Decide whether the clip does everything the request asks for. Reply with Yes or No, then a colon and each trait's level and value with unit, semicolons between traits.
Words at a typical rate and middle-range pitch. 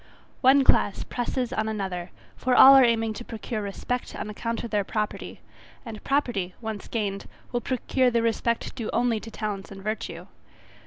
No: average, 170 wpm; high, 225 Hz